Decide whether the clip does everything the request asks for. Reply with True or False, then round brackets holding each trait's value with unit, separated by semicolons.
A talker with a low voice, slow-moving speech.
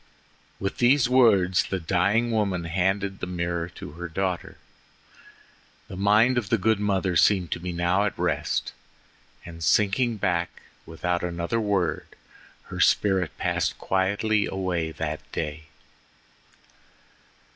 True (95 Hz; 125 wpm)